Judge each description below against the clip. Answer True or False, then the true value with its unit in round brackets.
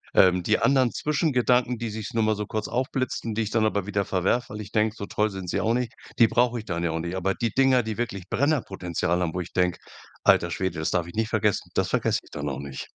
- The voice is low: True (105 Hz)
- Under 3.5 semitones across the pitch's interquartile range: False (4.7 semitones)